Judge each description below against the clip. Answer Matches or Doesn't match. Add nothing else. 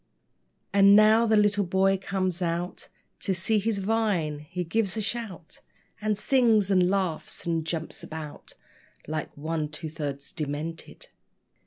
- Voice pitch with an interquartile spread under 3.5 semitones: Doesn't match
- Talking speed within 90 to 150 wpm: Matches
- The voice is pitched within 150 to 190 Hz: Matches